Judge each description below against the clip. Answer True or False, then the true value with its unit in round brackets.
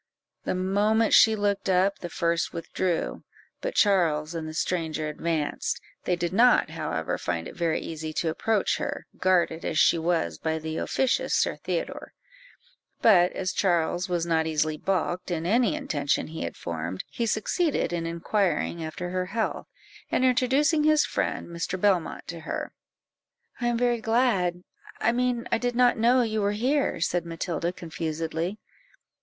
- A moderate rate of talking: True (160 wpm)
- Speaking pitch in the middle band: True (180 Hz)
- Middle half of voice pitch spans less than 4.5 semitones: False (5.4 semitones)